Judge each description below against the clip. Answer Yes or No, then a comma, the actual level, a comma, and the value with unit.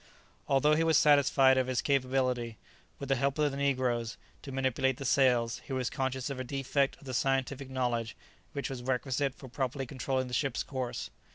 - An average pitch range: No, narrow, 1.5 semitones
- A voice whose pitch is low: Yes, low, 130 Hz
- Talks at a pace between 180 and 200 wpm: Yes, average, 190 wpm